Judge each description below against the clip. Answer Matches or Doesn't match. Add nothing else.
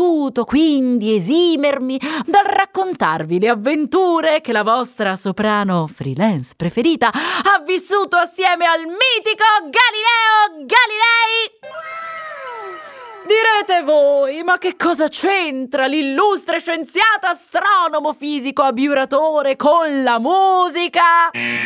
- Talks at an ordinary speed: Doesn't match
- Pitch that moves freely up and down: Matches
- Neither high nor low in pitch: Doesn't match